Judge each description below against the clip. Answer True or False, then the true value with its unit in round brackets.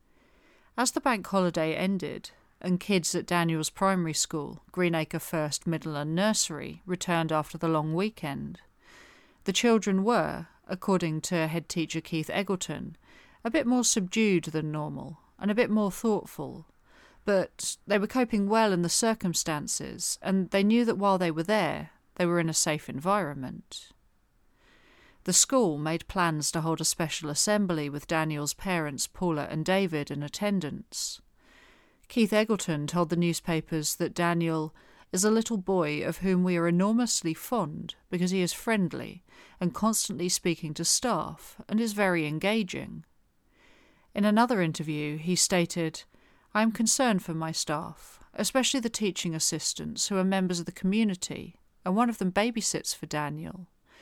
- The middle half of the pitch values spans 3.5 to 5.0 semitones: True (4.4 semitones)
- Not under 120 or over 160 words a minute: True (150 wpm)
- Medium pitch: True (180 Hz)